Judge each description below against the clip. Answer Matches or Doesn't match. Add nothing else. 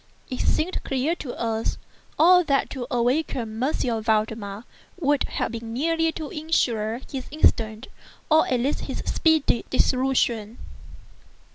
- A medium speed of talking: Doesn't match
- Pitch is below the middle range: Doesn't match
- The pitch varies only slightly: Doesn't match